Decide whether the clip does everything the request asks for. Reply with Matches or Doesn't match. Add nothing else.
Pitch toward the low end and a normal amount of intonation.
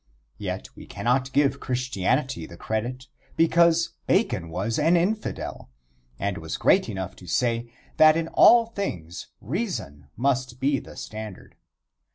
Doesn't match